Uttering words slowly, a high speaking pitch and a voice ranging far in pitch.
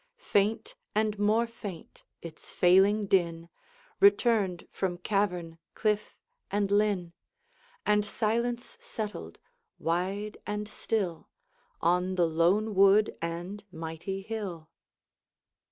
No: slow, 100 wpm; high, 200 Hz; average, 3.3 semitones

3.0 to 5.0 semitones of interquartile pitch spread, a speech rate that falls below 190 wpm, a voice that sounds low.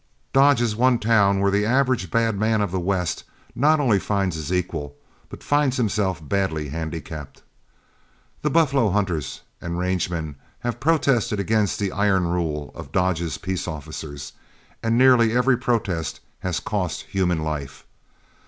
No: wide, 5.6 semitones; average, 150 wpm; low, 100 Hz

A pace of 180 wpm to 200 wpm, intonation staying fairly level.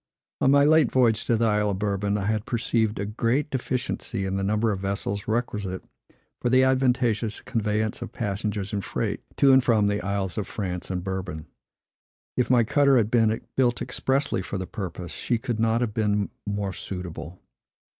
No: average, 185 wpm; average, 3.5 semitones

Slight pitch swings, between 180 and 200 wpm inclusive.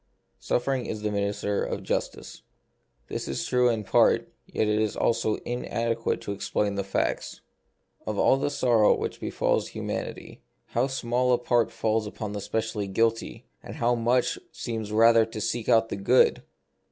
No: narrow, 2.3 semitones; average, 165 wpm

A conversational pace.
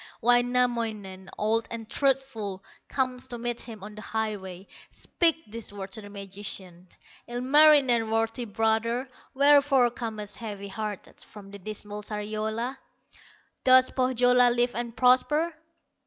No: slow, 125 wpm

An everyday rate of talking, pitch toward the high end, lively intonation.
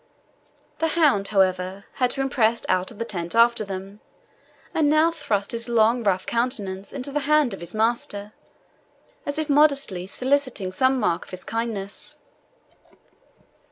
Yes: average, 145 wpm; high, 230 Hz; wide, 5.8 semitones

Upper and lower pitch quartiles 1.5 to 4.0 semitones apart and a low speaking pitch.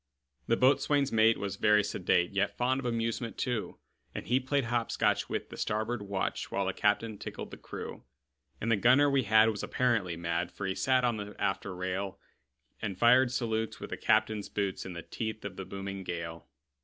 Yes: average, 3.6 semitones; low, 110 Hz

